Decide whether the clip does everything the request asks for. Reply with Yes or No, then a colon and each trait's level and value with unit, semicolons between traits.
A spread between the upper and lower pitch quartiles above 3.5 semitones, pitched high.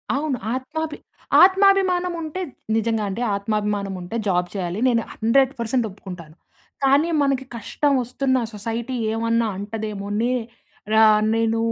Yes: average, 4.8 semitones; high, 230 Hz